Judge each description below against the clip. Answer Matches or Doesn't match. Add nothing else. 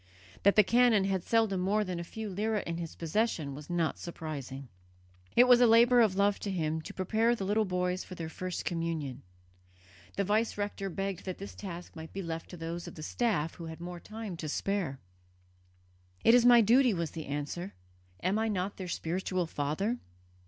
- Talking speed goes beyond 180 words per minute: Matches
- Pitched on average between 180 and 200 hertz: Matches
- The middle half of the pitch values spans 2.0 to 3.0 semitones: Doesn't match